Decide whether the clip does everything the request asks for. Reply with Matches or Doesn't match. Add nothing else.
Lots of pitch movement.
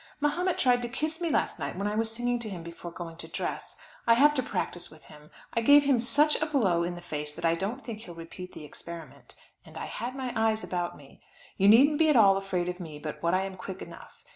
Matches